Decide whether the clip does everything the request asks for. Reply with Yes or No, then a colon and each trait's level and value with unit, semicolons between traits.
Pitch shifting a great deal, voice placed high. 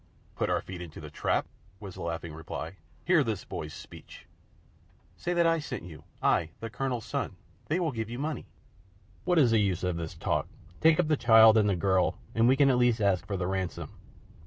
No: wide, 7.0 semitones; low, 110 Hz